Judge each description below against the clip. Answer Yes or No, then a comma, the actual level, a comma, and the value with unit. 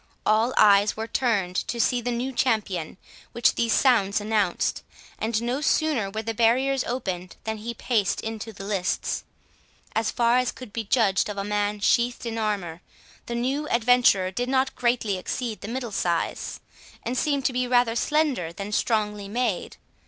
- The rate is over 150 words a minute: Yes, average, 170 wpm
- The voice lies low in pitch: No, high, 225 Hz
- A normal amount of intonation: Yes, average, 3.3 semitones